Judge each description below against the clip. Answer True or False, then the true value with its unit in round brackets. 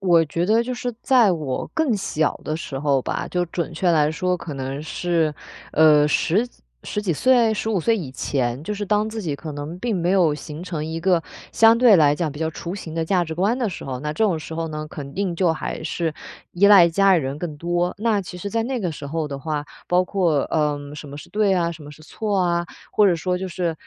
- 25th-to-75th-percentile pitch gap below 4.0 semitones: False (4.4 semitones)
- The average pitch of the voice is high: False (170 Hz)